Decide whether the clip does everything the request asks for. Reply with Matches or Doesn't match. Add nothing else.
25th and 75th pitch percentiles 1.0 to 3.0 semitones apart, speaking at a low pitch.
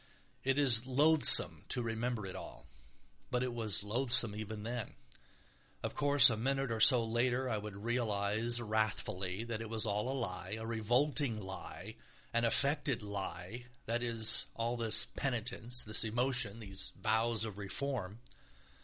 Matches